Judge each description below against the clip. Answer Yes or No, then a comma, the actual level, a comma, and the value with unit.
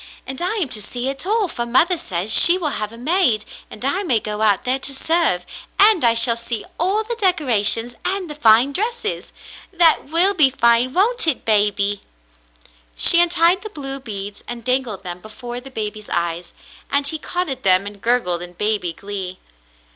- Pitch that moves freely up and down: Yes, wide, 8.3 semitones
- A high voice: Yes, very high, 250 Hz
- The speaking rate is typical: Yes, average, 190 wpm